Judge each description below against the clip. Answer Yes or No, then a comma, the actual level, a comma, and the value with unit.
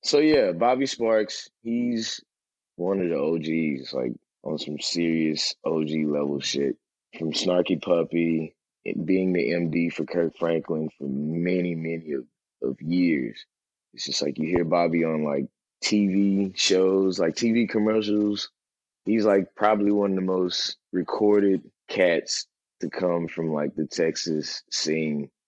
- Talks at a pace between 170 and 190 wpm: No, average, 145 wpm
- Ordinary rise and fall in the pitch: Yes, average, 4.1 semitones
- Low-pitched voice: Yes, very low, 85 Hz